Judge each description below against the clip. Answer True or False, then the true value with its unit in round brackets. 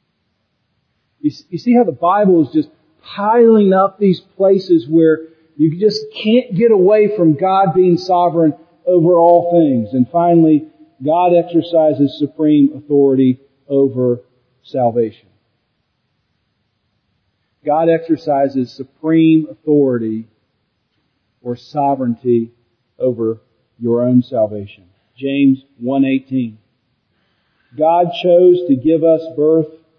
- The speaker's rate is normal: False (100 wpm)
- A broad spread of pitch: True (5.9 semitones)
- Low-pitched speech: False (155 Hz)